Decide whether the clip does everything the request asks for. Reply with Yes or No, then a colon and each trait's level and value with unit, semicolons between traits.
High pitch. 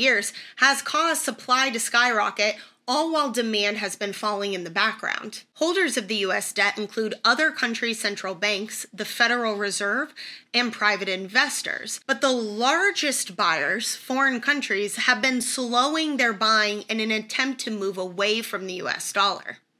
Yes: high, 225 Hz